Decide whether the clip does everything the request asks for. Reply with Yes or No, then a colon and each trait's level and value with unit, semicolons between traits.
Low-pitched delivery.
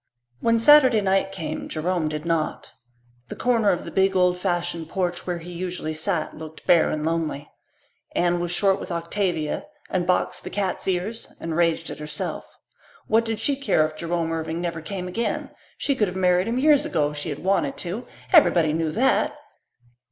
No: medium, 175 Hz